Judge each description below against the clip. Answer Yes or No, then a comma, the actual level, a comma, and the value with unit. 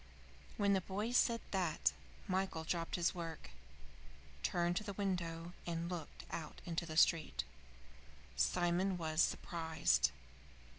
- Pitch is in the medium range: Yes, medium, 175 Hz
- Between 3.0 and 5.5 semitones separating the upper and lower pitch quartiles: No, narrow, 2.4 semitones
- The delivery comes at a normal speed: No, slow, 120 wpm